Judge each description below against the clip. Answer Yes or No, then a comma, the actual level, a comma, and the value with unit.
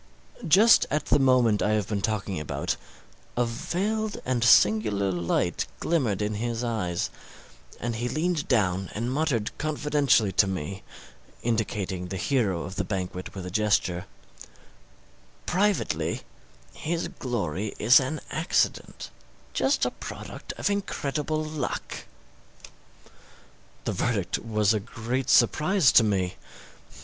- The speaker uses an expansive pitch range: Yes, wide, 6.6 semitones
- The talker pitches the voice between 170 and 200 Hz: No, low, 115 Hz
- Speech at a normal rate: No, slow, 125 wpm